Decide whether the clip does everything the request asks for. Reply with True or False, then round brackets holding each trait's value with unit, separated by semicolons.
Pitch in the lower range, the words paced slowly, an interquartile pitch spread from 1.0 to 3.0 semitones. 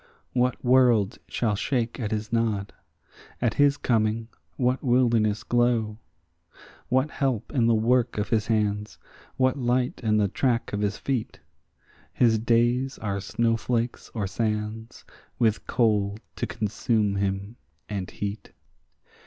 True (115 Hz; 130 wpm; 2.6 semitones)